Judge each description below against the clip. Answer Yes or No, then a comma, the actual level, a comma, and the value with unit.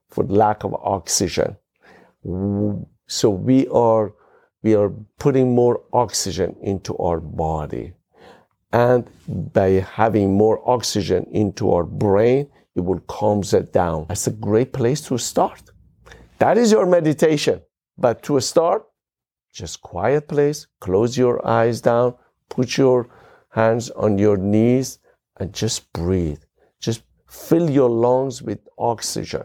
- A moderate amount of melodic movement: Yes, average, 4.3 semitones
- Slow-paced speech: Yes, slow, 130 wpm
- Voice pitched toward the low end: Yes, low, 110 Hz